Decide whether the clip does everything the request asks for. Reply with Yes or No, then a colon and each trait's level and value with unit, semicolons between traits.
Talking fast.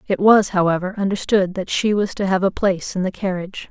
Yes: fast, 225 wpm